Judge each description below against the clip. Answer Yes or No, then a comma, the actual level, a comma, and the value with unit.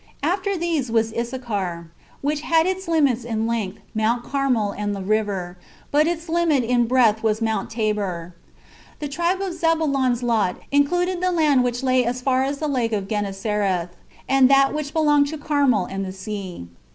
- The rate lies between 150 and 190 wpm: Yes, average, 175 wpm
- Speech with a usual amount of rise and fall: No, wide, 6.0 semitones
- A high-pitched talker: Yes, very high, 250 Hz